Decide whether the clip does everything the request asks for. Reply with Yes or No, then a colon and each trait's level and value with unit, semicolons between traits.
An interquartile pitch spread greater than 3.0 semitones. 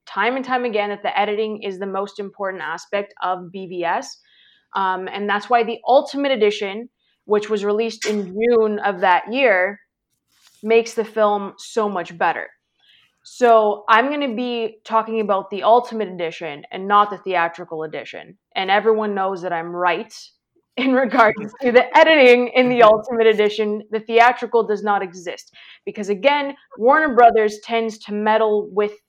No: narrow, 2.6 semitones